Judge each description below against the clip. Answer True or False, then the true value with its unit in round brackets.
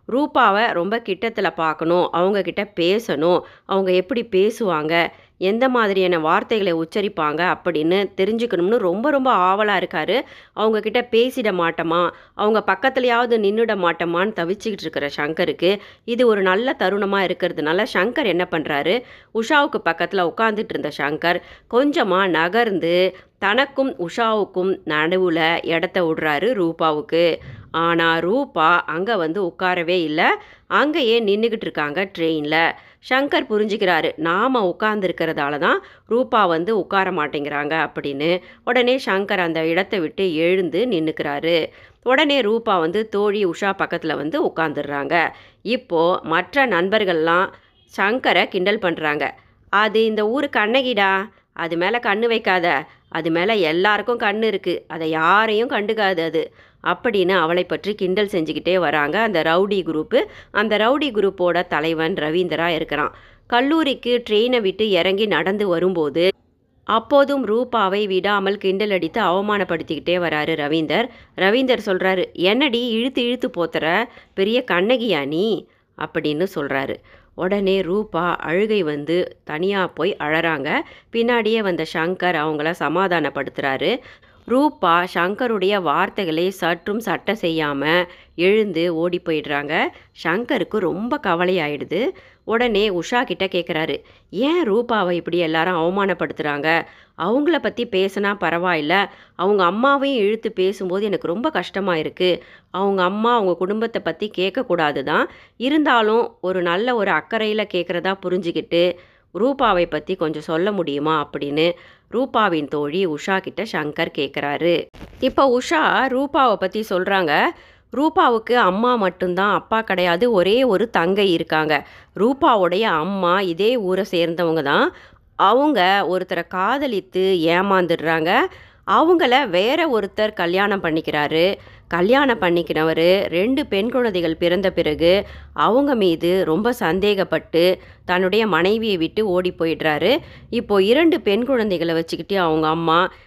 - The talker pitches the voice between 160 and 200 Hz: True (185 Hz)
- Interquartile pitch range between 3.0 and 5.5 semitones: True (4.6 semitones)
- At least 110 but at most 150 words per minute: True (115 wpm)